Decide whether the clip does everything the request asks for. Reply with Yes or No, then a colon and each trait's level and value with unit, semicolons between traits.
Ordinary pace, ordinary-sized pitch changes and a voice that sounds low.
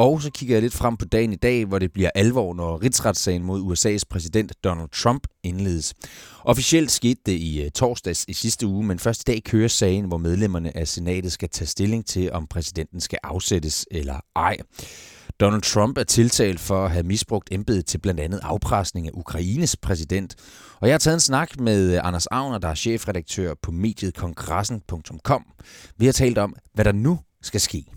Yes: average, 195 wpm; average, 4.4 semitones; very low, 95 Hz